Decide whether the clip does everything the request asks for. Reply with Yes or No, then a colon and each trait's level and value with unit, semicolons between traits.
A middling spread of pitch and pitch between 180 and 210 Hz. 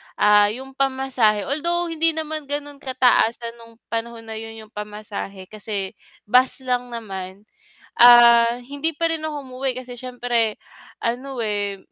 No: average, 3.8 semitones; high, 240 Hz